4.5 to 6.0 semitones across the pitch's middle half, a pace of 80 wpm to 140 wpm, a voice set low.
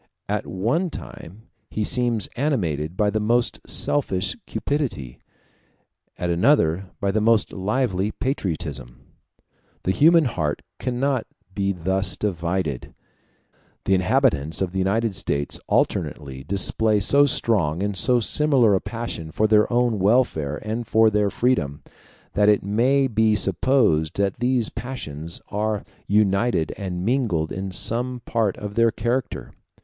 Yes: average, 4.9 semitones; slow, 135 wpm; low, 105 Hz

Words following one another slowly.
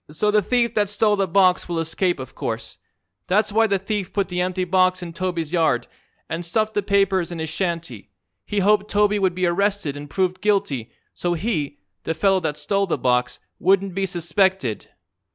No: average, 190 wpm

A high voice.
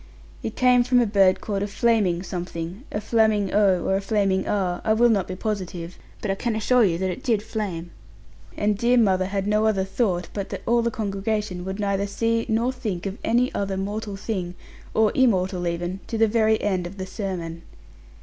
Yes: high, 200 Hz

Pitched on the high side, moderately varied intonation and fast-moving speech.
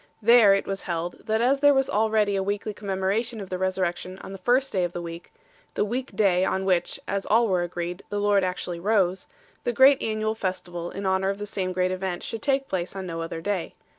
Yes: high, 195 Hz; average, 3.0 semitones; fast, 230 wpm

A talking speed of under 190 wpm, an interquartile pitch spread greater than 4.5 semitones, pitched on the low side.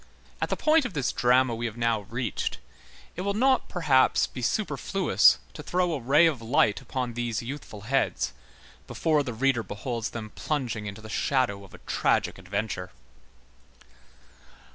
Yes: average, 165 wpm; average, 5.0 semitones; low, 125 Hz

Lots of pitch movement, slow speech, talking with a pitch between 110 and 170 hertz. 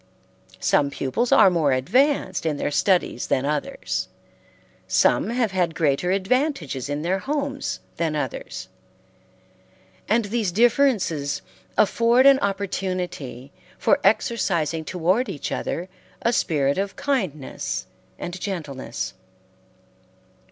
No: wide, 7.6 semitones; slow, 110 wpm; medium, 185 Hz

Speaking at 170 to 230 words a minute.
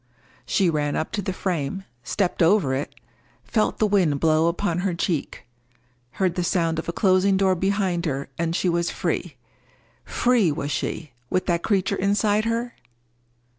No: average, 160 wpm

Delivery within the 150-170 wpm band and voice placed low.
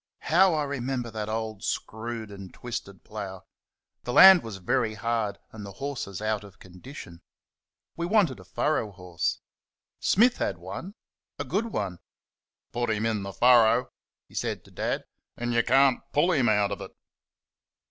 Yes: average, 160 wpm; low, 115 Hz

